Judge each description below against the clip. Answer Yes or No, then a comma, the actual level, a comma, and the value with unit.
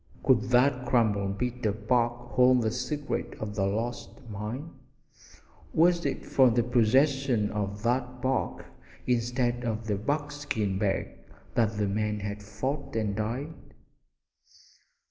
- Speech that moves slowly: Yes, slow, 130 wpm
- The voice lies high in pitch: No, low, 120 Hz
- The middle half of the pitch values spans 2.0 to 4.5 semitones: Yes, average, 3.3 semitones